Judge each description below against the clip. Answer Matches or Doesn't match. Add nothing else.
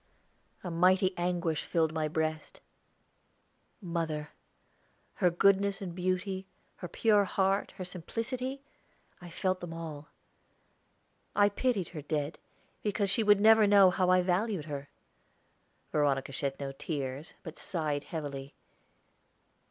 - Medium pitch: Matches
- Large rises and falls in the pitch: Doesn't match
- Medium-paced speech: Doesn't match